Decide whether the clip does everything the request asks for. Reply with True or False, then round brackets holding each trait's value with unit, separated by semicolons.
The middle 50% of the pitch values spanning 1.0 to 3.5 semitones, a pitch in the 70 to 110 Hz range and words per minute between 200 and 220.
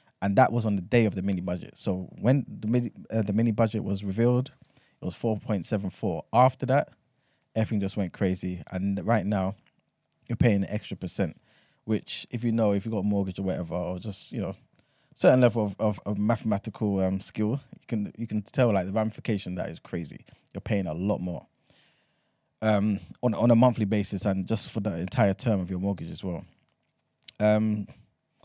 True (2.9 semitones; 105 Hz; 205 wpm)